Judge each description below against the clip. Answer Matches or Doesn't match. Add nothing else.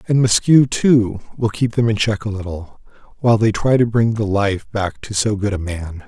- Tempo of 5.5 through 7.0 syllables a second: Doesn't match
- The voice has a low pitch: Matches